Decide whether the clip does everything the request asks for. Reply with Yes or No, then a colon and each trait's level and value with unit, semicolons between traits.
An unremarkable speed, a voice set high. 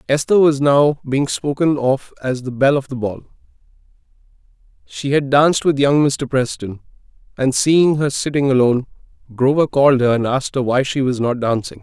No: average, 180 wpm; low, 135 Hz